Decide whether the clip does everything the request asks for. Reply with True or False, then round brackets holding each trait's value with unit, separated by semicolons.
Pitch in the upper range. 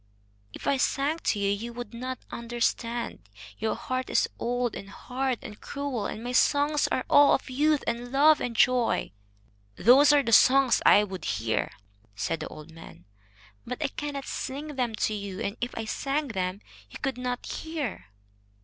True (245 Hz)